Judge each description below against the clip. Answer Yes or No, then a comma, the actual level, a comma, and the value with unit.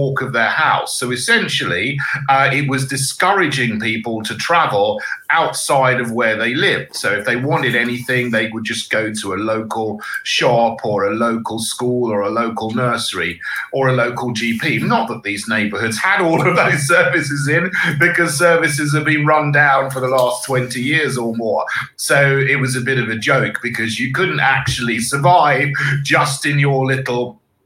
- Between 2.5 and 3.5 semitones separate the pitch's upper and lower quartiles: No, average, 3.9 semitones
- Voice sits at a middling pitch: No, low, 130 Hz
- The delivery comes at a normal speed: Yes, average, 180 wpm